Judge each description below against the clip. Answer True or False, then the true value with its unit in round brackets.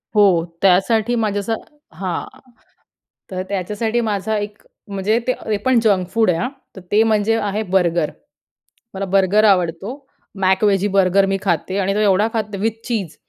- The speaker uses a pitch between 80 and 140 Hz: False (200 Hz)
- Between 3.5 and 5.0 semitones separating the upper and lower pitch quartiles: False (2.5 semitones)